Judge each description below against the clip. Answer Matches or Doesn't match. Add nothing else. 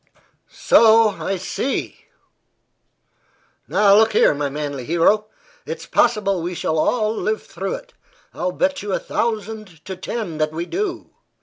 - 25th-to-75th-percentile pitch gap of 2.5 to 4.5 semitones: Doesn't match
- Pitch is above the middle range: Matches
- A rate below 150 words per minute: Matches